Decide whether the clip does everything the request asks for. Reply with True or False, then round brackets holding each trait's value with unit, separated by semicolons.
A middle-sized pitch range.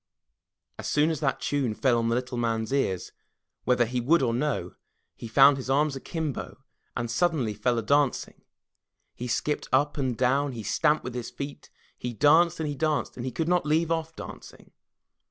True (3.8 semitones)